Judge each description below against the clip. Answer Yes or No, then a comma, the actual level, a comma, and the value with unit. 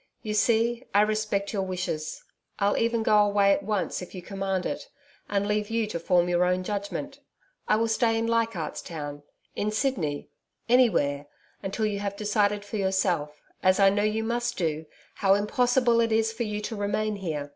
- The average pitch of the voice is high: Yes, high, 205 Hz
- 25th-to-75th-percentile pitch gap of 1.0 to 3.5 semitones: Yes, average, 3.0 semitones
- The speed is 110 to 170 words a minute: No, average, 185 wpm